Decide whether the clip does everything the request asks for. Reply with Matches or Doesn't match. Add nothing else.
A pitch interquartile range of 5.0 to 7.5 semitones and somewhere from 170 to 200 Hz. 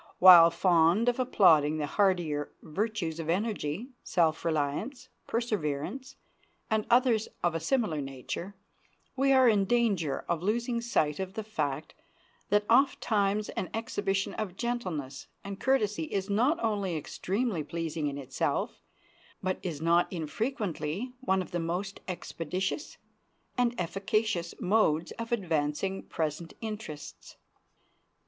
Matches